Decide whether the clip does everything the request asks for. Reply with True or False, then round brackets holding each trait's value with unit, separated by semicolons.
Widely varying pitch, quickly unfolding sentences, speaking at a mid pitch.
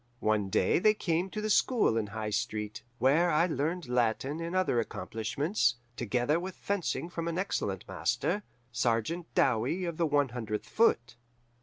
False (7.4 semitones; 160 wpm; 145 Hz)